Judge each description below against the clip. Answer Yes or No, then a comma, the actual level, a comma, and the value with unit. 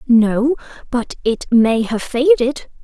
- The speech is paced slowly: Yes, slow, 125 wpm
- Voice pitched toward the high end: Yes, high, 240 Hz